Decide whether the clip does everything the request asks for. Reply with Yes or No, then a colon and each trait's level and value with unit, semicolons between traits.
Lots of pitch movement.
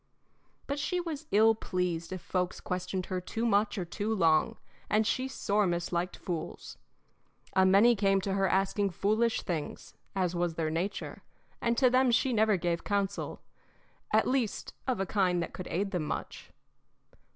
No: average, 3.6 semitones